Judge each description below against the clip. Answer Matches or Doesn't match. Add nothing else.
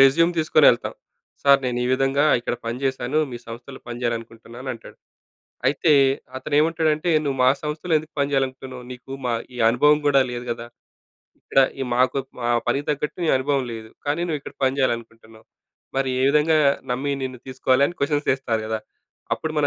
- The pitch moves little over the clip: Doesn't match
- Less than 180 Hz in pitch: Matches